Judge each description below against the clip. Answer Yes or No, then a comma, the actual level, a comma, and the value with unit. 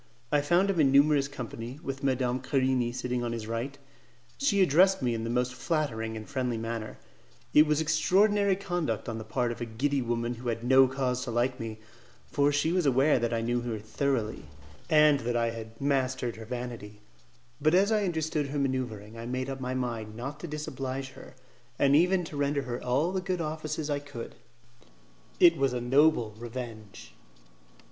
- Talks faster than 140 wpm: Yes, average, 190 wpm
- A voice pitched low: Yes, low, 130 Hz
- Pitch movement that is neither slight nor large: Yes, average, 4.2 semitones